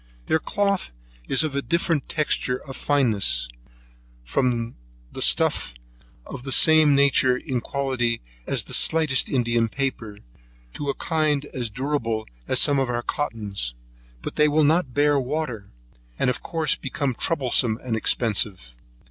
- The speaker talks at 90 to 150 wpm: Yes, average, 140 wpm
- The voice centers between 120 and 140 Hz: Yes, low, 135 Hz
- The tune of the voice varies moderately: Yes, average, 4.1 semitones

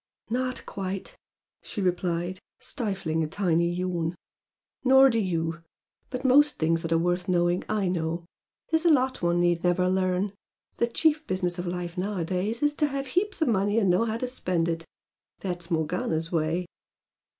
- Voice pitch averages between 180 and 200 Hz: Yes, medium, 185 Hz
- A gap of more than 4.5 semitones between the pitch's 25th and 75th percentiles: Yes, average, 5.2 semitones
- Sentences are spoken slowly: No, average, 165 wpm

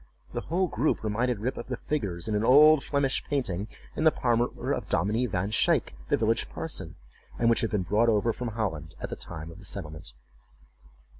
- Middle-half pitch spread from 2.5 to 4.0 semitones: No, average, 4.7 semitones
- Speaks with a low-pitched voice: Yes, low, 110 Hz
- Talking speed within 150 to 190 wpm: No, average, 200 wpm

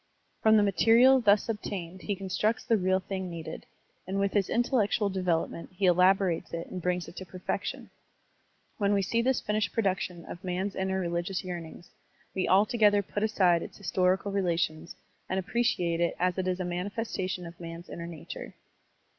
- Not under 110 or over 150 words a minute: No, average, 180 wpm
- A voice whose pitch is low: No, high, 190 Hz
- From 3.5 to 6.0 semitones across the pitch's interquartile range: No, narrow, 2.6 semitones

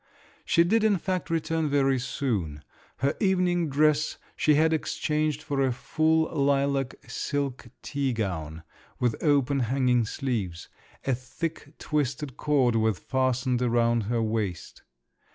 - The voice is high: No, low, 135 Hz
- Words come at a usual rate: No, slow, 130 wpm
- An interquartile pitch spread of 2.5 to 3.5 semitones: No, average, 4.3 semitones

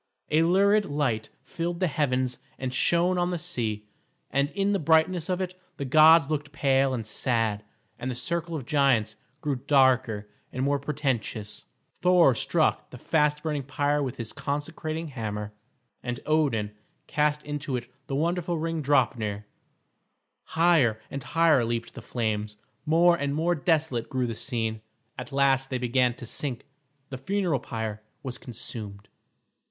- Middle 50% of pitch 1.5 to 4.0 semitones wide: No, average, 4.9 semitones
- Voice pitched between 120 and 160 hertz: Yes, medium, 140 Hz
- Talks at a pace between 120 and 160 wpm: Yes, average, 155 wpm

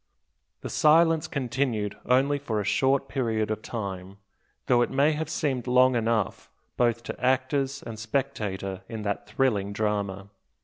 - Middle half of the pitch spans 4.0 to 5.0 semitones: Yes, average, 4.4 semitones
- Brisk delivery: No, average, 145 wpm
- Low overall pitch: Yes, low, 120 Hz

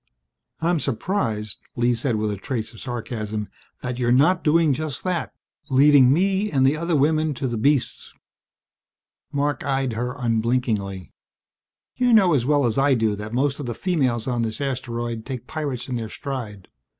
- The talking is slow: No, average, 170 wpm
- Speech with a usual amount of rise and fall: Yes, average, 4.2 semitones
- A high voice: No, low, 130 Hz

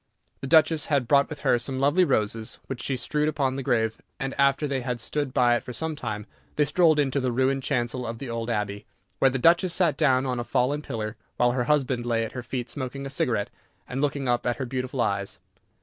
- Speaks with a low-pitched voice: Yes, low, 130 Hz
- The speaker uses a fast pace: Yes, fast, 230 wpm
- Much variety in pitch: No, average, 2.8 semitones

